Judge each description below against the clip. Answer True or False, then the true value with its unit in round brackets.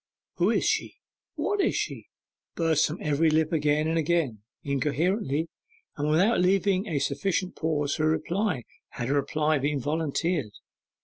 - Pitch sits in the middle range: True (155 Hz)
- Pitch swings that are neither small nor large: True (3.0 semitones)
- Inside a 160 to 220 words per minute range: False (150 wpm)